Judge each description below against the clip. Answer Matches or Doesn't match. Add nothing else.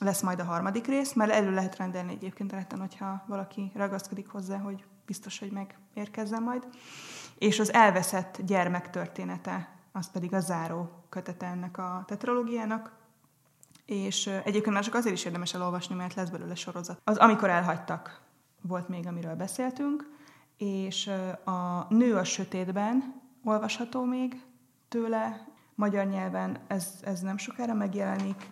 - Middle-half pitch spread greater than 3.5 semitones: Doesn't match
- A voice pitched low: Doesn't match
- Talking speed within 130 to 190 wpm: Matches